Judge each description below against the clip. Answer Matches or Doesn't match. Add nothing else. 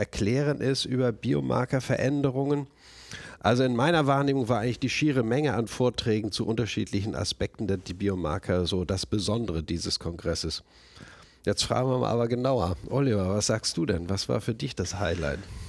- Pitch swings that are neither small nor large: Doesn't match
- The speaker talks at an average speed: Matches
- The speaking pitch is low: Matches